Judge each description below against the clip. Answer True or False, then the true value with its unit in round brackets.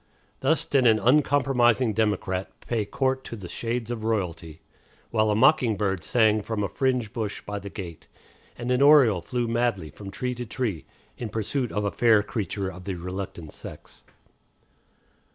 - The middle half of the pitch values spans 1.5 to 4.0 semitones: True (3.7 semitones)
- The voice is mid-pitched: False (110 Hz)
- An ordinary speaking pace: True (170 wpm)